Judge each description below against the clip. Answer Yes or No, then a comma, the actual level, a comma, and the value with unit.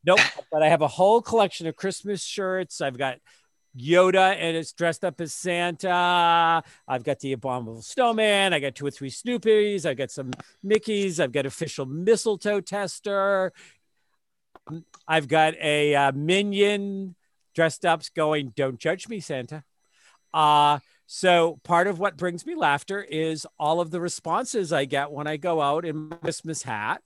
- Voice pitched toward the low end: No, medium, 165 Hz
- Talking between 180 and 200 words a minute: No, average, 160 wpm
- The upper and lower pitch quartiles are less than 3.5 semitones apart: No, average, 4.6 semitones